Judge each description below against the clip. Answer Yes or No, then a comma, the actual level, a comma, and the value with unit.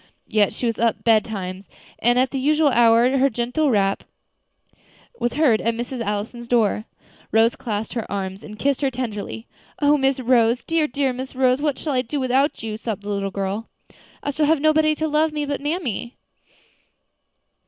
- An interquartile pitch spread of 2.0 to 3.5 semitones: No, average, 4.2 semitones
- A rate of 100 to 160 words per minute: No, average, 190 wpm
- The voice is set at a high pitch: Yes, high, 245 Hz